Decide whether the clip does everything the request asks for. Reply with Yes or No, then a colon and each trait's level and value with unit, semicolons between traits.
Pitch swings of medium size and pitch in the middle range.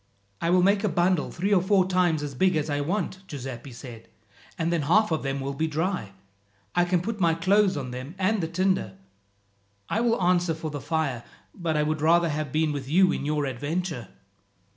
Yes: average, 4.2 semitones; medium, 165 Hz